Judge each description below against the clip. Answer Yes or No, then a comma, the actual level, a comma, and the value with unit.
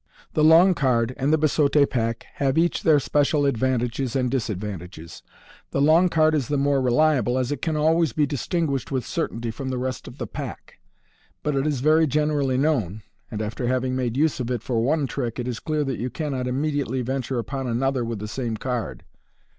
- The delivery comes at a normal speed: No, fast, 215 wpm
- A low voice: Yes, low, 130 Hz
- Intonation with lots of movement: No, average, 3.7 semitones